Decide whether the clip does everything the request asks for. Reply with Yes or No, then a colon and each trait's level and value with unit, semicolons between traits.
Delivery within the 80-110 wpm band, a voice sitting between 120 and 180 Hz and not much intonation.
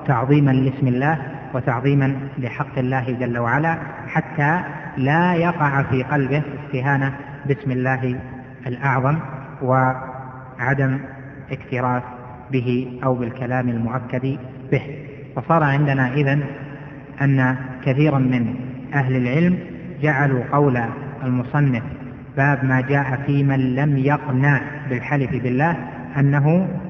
Yes: average, 100 wpm; low, 135 Hz; narrow, 1.7 semitones